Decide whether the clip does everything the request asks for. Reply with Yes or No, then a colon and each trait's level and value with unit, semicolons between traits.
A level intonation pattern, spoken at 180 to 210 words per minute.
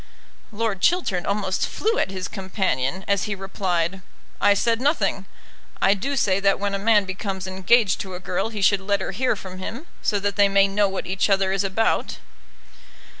Yes: narrow, 1.6 semitones; average, 190 wpm